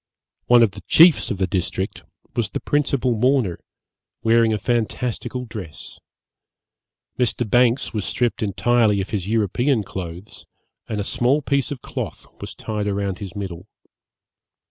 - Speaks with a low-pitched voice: Yes, low, 110 Hz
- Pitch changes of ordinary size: Yes, average, 3.7 semitones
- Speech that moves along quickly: No, average, 145 wpm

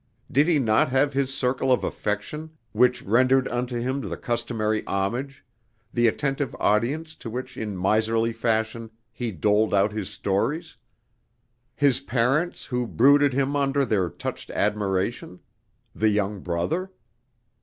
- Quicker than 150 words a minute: No, slow, 135 wpm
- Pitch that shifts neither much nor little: Yes, average, 4.2 semitones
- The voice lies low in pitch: Yes, low, 120 Hz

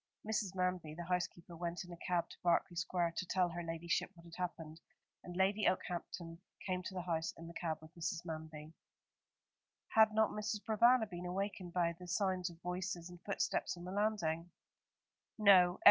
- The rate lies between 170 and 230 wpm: Yes, average, 180 wpm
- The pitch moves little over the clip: Yes, narrow, 2.0 semitones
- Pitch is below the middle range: No, medium, 180 Hz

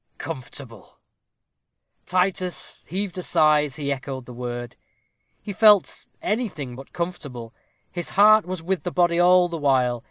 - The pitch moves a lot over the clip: Yes, wide, 5.8 semitones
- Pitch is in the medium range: Yes, medium, 165 Hz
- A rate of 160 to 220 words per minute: No, average, 145 wpm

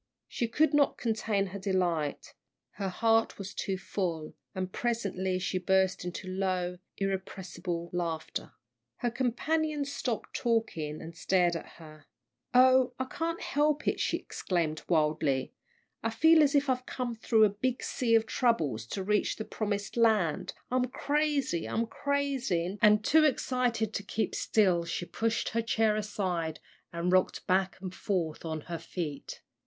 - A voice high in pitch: Yes, high, 200 Hz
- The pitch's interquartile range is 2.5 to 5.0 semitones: No, wide, 5.4 semitones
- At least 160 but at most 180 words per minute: No, average, 150 wpm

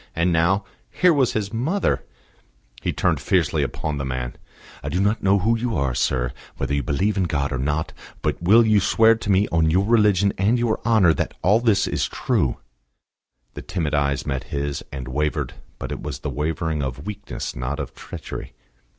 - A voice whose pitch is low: Yes, very low, 85 Hz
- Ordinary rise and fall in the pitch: No, wide, 6.8 semitones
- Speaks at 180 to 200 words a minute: Yes, average, 195 wpm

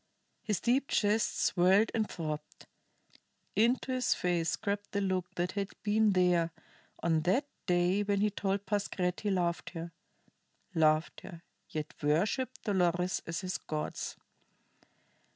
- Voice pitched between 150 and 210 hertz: Yes, medium, 185 Hz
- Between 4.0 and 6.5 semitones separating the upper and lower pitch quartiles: No, average, 3.3 semitones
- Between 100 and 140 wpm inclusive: Yes, slow, 135 wpm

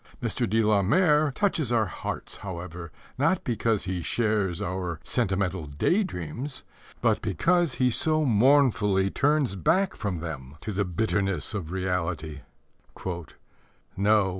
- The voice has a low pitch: Yes, low, 100 Hz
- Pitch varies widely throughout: Yes, wide, 6.5 semitones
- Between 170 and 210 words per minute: No, slow, 135 wpm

